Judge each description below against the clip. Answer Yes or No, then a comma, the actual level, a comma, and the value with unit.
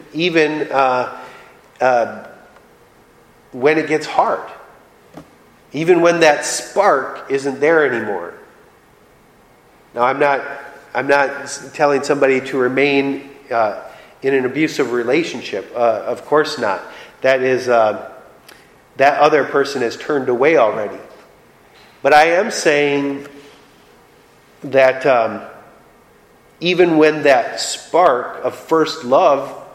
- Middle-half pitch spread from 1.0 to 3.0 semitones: Yes, narrow, 2.4 semitones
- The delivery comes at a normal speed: No, slow, 110 wpm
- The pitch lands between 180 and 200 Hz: No, medium, 140 Hz